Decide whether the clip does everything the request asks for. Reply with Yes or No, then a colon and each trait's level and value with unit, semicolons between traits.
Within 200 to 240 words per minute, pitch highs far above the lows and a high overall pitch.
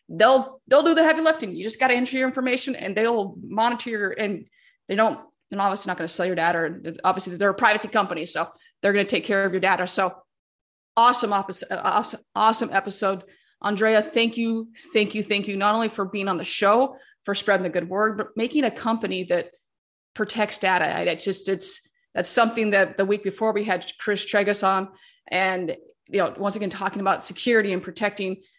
No: fast, 205 wpm; average, 3.1 semitones; high, 205 Hz